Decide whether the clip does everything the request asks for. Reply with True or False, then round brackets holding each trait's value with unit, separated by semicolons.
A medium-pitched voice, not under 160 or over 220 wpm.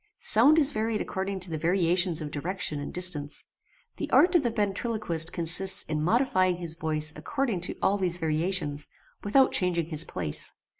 True (180 Hz; 165 wpm)